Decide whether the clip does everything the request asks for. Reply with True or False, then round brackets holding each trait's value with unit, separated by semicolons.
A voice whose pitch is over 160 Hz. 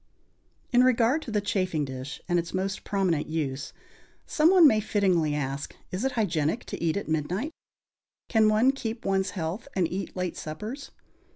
True (190 Hz)